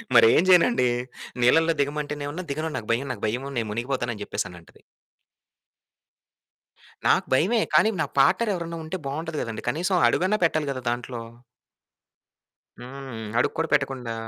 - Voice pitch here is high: No, medium, 140 Hz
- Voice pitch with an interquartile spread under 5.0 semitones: No, average, 5.3 semitones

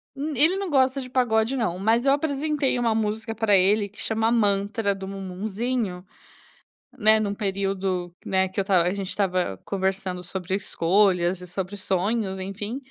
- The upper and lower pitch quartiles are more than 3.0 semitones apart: Yes, average, 3.4 semitones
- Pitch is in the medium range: No, high, 200 Hz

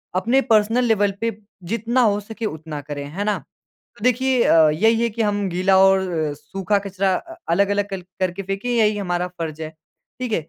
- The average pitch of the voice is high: Yes, high, 200 Hz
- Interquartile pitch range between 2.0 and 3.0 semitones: No, average, 3.6 semitones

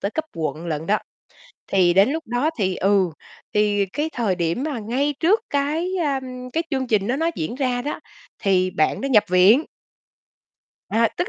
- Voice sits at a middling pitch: No, high, 230 Hz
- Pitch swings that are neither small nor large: No, wide, 7.0 semitones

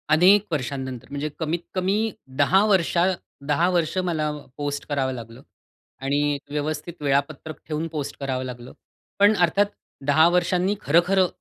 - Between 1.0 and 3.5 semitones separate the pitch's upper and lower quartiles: No, average, 3.9 semitones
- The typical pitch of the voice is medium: Yes, medium, 155 Hz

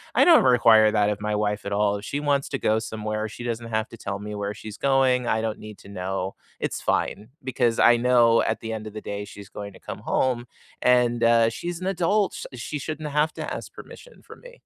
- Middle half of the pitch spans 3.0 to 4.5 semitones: Yes, average, 3.6 semitones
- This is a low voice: Yes, low, 115 Hz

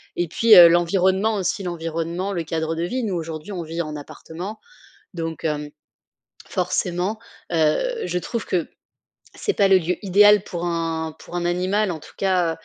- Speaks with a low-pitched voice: No, medium, 175 Hz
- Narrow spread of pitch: No, average, 3.0 semitones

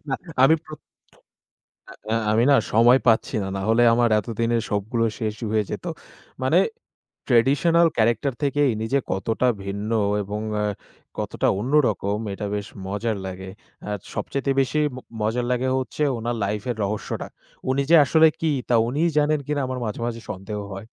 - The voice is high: No, low, 115 Hz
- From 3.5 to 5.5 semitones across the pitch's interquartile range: Yes, average, 4.2 semitones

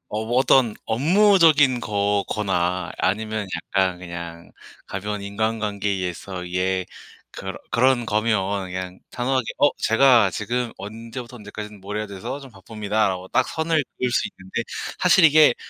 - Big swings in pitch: No, average, 4.5 semitones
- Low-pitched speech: Yes, low, 105 Hz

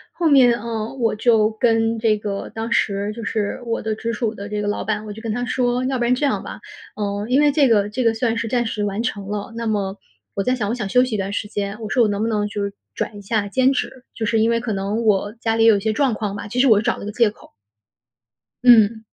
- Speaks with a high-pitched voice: Yes, high, 220 Hz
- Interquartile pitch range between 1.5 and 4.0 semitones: Yes, narrow, 2.4 semitones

